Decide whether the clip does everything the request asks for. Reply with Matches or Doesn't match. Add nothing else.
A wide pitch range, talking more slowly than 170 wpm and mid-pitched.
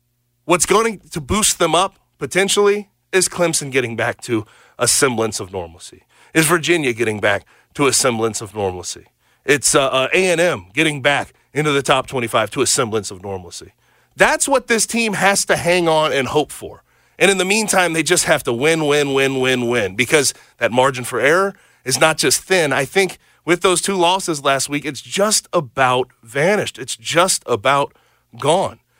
Doesn't match